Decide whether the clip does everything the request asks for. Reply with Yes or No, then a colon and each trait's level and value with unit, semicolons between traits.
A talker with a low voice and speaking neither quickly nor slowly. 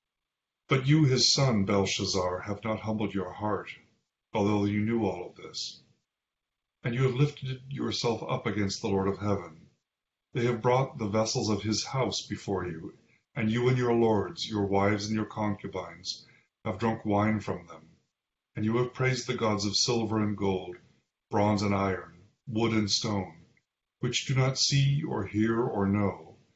Yes: low, 110 Hz; average, 170 wpm